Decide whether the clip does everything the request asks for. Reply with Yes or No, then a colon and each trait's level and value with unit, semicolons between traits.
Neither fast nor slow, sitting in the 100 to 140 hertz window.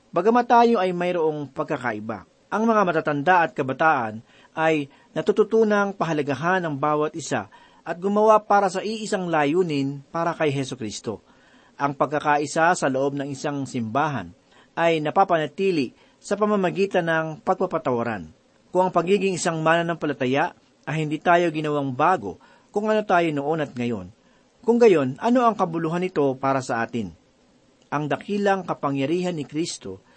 No: average, 140 wpm; medium, 160 Hz